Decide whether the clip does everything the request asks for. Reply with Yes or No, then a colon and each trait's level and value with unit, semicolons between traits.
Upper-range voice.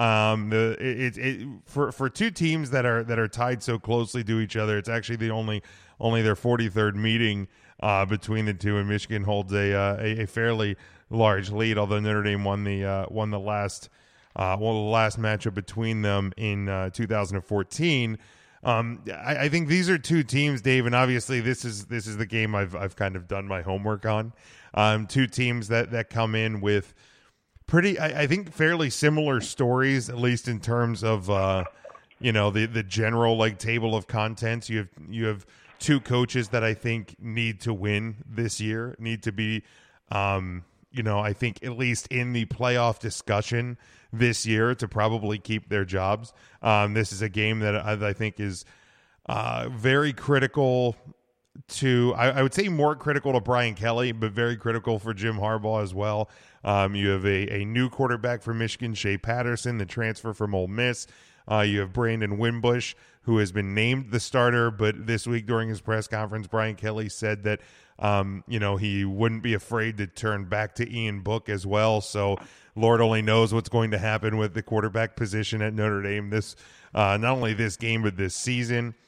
No: low, 110 Hz